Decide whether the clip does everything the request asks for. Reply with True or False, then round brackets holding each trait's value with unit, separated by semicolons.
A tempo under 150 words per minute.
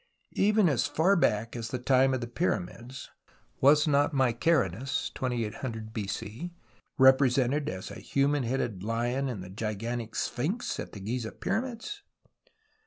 True (135 wpm)